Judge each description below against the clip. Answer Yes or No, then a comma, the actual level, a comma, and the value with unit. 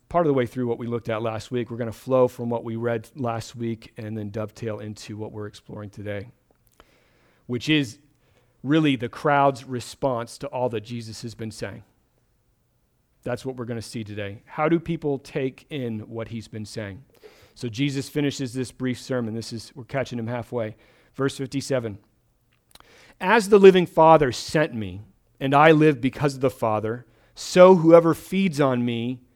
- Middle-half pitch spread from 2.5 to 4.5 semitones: Yes, average, 3.4 semitones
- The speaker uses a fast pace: No, average, 185 wpm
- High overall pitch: No, low, 125 Hz